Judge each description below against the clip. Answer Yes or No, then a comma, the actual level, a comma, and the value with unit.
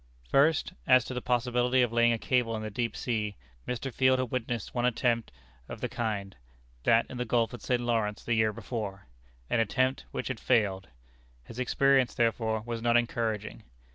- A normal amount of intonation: No, narrow, 2.1 semitones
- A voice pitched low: Yes, low, 120 Hz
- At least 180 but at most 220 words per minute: Yes, average, 185 wpm